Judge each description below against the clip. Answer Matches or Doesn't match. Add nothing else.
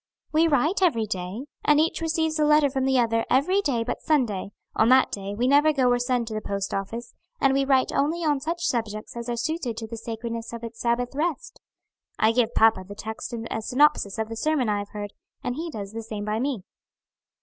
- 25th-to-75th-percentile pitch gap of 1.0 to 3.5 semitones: Doesn't match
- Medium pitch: Doesn't match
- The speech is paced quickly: Matches